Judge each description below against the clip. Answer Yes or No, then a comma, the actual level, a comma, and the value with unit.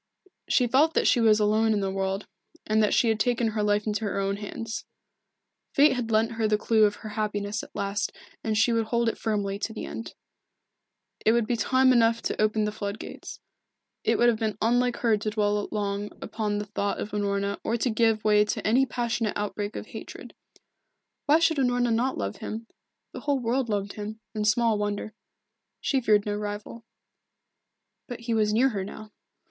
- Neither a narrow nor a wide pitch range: No, narrow, 2.0 semitones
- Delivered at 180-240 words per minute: Yes, average, 200 wpm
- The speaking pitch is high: Yes, high, 215 Hz